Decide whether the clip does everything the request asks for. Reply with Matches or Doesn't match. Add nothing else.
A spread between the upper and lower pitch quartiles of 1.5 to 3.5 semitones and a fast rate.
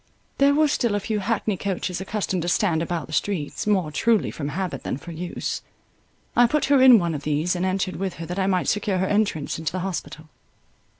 Doesn't match